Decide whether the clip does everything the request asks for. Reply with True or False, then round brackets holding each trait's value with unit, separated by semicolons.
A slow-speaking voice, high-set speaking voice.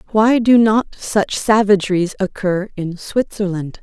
True (125 wpm; 200 Hz)